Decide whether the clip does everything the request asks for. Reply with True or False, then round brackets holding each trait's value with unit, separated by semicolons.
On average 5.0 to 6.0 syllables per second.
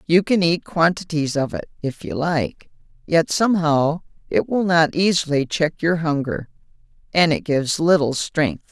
False (4.5 syllables/s)